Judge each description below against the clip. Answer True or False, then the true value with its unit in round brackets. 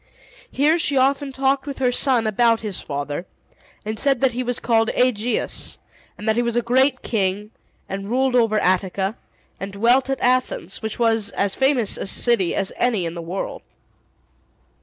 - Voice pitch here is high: True (230 Hz)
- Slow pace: False (175 wpm)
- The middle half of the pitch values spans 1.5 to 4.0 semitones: False (4.4 semitones)